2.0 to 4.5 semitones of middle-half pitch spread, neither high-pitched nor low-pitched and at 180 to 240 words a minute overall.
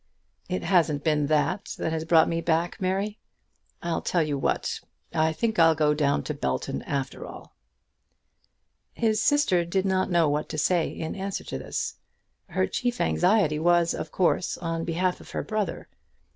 No: average, 3.3 semitones; medium, 170 Hz; average, 170 wpm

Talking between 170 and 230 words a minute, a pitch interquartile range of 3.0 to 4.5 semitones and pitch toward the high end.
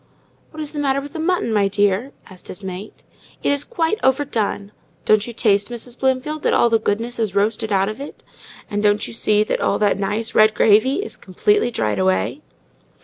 No: average, 200 wpm; average, 5.0 semitones; high, 220 Hz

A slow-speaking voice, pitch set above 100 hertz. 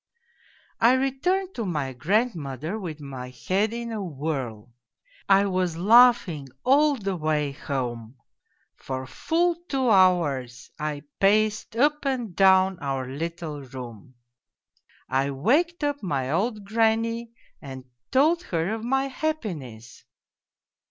Yes: slow, 125 wpm; medium, 185 Hz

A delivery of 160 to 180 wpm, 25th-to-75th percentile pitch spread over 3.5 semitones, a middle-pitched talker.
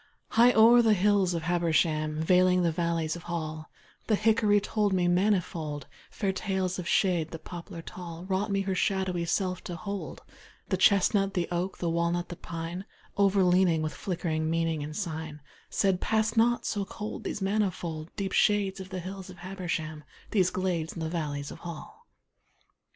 No: average, 170 wpm; average, 3.0 semitones; medium, 180 Hz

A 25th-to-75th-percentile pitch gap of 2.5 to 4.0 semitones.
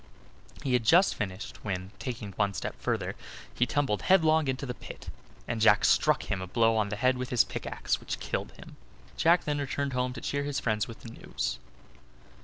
No: average, 5.1 semitones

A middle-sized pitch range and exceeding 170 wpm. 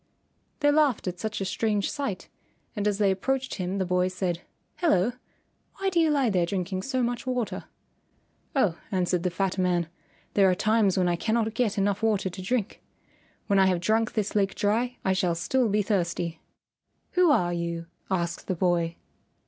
Yes: average, 3.9 semitones; average, 180 wpm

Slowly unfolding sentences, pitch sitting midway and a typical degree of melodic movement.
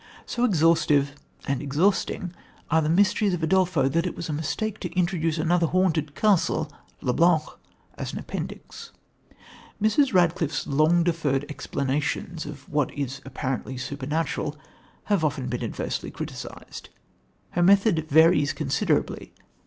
Yes: slow, 130 wpm; medium, 160 Hz; average, 3.6 semitones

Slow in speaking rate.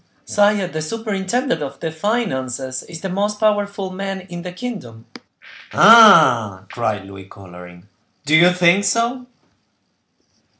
Yes: slow, 125 wpm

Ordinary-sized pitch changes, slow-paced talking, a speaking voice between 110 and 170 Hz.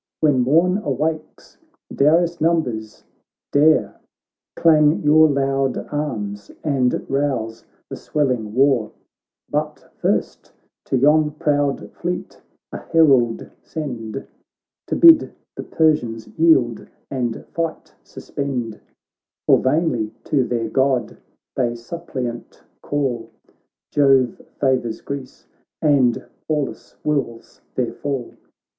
Yes: average, 4.0 semitones; slow, 100 wpm; low, 135 Hz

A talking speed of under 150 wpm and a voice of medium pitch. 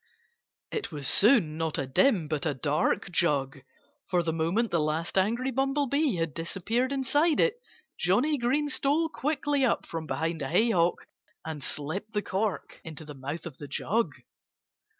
No: average, 160 wpm; medium, 180 Hz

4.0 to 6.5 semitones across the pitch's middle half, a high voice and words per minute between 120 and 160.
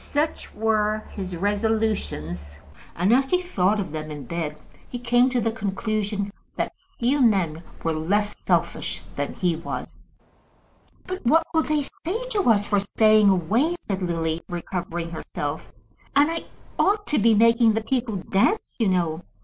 Yes: wide, 5.6 semitones; high, 210 Hz; average, 155 wpm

